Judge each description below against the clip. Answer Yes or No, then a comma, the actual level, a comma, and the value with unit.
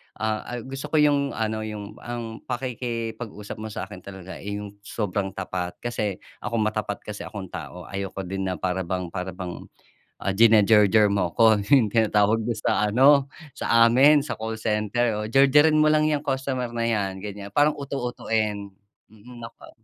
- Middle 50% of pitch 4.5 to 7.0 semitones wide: No, average, 3.3 semitones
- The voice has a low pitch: Yes, low, 110 Hz